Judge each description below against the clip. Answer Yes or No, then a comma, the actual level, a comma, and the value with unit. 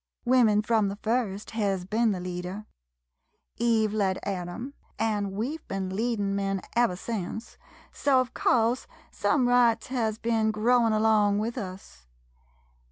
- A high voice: Yes, high, 215 Hz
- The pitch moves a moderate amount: Yes, average, 3.1 semitones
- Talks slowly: No, average, 145 wpm